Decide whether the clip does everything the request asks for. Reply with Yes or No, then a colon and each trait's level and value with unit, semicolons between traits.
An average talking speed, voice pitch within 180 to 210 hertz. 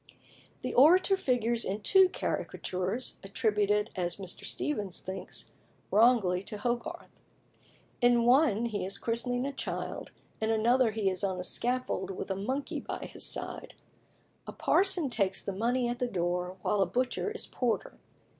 No: average, 155 wpm; high, 225 Hz